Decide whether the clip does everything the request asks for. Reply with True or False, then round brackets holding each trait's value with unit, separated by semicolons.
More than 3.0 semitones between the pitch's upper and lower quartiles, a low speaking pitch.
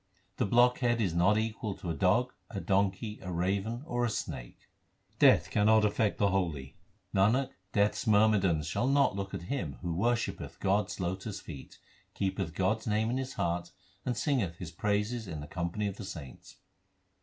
True (3.9 semitones; 100 Hz)